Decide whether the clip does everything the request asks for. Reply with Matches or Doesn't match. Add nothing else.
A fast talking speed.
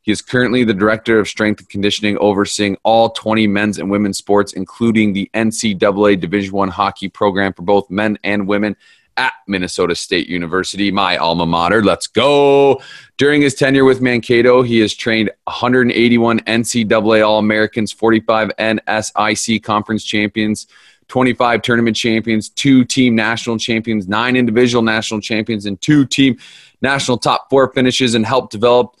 Doesn't match